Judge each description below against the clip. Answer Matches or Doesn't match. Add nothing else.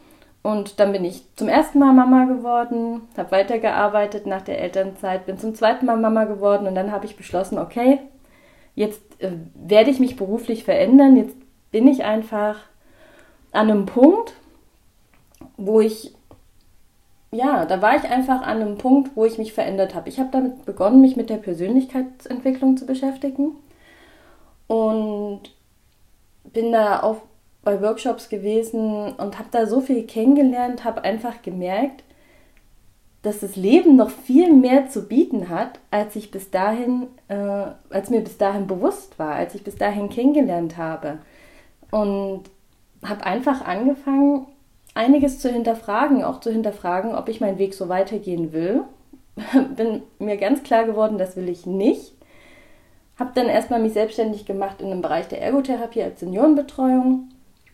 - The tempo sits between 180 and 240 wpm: Doesn't match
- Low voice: Doesn't match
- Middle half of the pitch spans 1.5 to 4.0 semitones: Doesn't match